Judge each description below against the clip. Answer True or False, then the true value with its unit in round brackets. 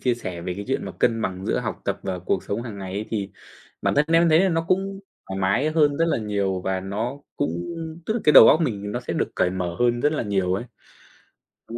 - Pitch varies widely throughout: True (7.3 semitones)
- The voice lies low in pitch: True (110 Hz)